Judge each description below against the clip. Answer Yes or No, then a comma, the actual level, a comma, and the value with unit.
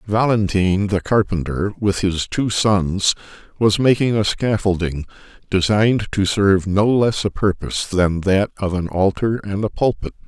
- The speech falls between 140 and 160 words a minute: Yes, average, 150 wpm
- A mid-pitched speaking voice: No, low, 100 Hz